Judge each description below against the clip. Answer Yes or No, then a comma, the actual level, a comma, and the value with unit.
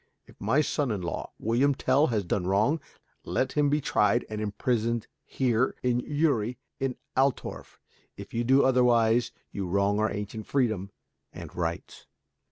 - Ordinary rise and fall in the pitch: Yes, average, 4.2 semitones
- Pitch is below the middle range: Yes, low, 120 Hz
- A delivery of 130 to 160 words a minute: Yes, average, 155 wpm